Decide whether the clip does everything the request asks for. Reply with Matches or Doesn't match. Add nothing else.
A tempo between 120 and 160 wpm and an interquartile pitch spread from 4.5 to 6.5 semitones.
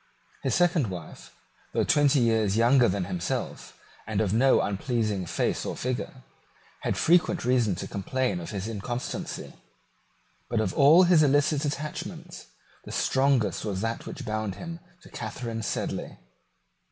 Matches